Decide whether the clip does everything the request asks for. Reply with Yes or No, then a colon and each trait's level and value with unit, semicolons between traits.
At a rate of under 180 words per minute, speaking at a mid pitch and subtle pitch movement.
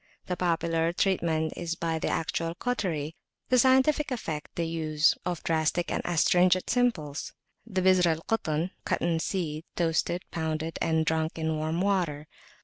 Yes: average, 150 wpm; medium, 165 Hz; narrow, 2.3 semitones